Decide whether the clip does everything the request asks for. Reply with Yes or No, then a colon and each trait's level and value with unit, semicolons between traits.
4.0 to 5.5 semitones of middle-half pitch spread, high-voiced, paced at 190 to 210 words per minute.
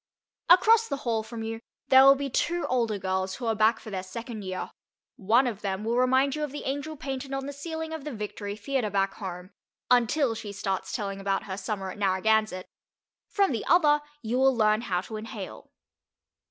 Yes: average, 5.1 semitones; high, 225 Hz; average, 200 wpm